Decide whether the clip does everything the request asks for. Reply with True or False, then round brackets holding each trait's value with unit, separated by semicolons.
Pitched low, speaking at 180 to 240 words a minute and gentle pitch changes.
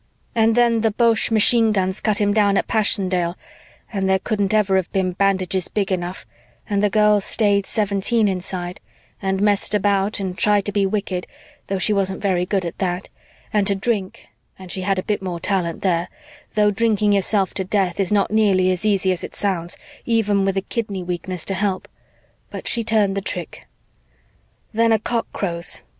False (195 Hz; 185 wpm; 2.1 semitones)